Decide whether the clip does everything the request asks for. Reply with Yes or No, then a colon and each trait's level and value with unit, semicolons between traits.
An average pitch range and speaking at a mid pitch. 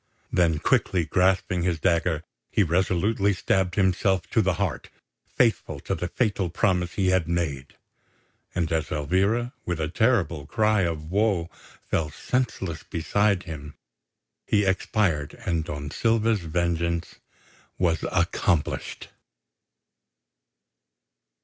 No: average, 3.3 semitones; very low, 90 Hz